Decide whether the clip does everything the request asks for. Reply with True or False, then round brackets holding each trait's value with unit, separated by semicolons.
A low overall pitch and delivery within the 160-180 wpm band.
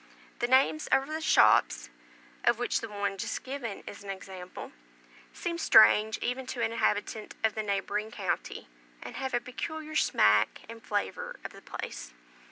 False (220 Hz; 165 wpm)